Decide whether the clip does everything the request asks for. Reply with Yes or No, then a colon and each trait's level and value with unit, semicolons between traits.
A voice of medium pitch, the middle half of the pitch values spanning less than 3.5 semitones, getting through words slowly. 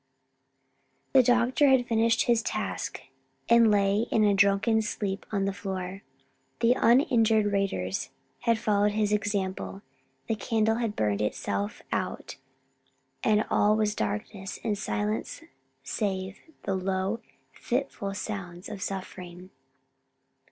No: high, 205 Hz; average, 2.9 semitones; slow, 120 wpm